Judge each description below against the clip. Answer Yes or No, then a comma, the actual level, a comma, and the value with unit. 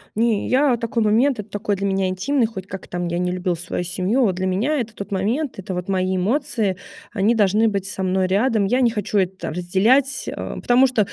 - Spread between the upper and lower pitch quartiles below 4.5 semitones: Yes, average, 3.8 semitones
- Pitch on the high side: Yes, high, 200 Hz